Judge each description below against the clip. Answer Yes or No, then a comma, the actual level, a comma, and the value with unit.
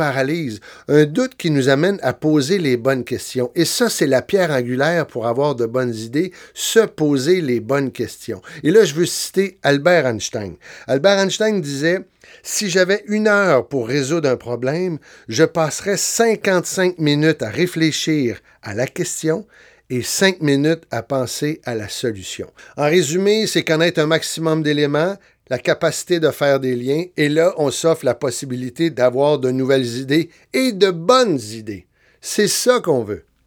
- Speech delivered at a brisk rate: No, average, 165 wpm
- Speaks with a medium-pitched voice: Yes, medium, 155 Hz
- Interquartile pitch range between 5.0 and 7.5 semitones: Yes, wide, 5.4 semitones